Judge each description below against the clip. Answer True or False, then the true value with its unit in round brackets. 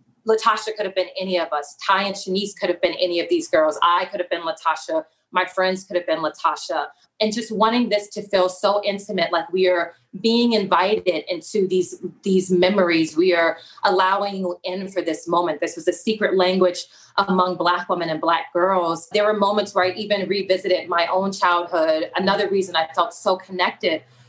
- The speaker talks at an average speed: True (195 wpm)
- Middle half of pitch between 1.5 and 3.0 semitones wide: True (2.5 semitones)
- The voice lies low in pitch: False (185 Hz)